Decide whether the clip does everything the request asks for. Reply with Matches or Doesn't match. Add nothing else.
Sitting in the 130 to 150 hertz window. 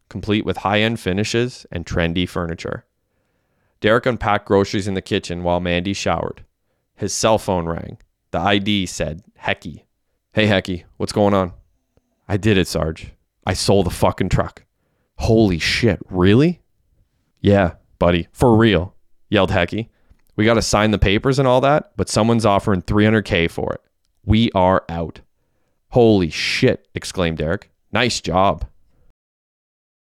Doesn't match